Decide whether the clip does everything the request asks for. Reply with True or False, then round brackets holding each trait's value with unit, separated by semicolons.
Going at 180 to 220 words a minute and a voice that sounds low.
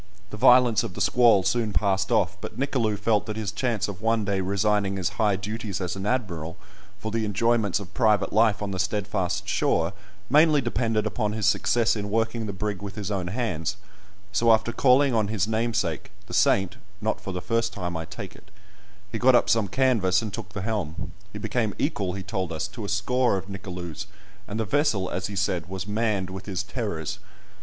True (205 wpm; 105 Hz)